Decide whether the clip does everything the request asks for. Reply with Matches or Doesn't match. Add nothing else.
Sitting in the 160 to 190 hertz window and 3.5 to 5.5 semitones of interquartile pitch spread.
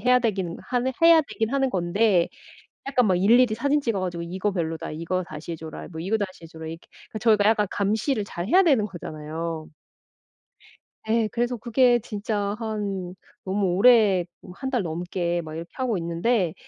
Doesn't match